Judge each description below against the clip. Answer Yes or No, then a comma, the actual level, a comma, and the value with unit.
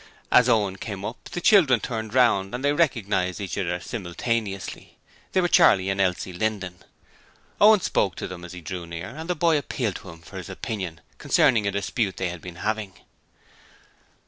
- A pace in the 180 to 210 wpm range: Yes, average, 185 wpm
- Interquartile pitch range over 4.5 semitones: Yes, average, 5.1 semitones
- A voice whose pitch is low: Yes, low, 100 Hz